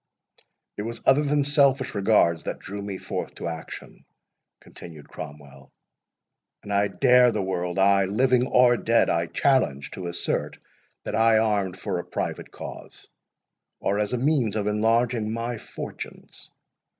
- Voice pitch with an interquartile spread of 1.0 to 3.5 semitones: No, average, 4.6 semitones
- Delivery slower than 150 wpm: Yes, average, 140 wpm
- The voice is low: Yes, low, 105 Hz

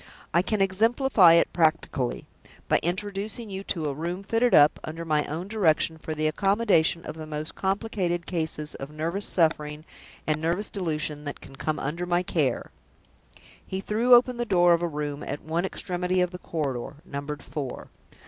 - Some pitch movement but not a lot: Yes, average, 4.1 semitones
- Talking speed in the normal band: Yes, average, 175 wpm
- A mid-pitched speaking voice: Yes, medium, 170 Hz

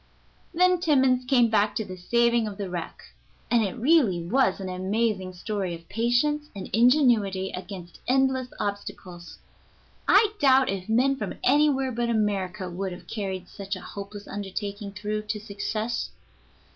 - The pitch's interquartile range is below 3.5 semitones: No, average, 4.7 semitones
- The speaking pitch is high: Yes, high, 210 Hz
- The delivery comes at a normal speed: Yes, average, 155 wpm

